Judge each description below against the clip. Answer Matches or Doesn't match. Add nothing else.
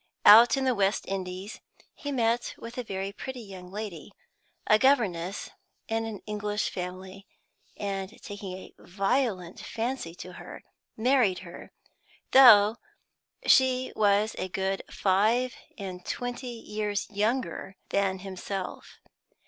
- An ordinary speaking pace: Doesn't match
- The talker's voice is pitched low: Doesn't match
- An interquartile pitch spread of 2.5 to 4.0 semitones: Matches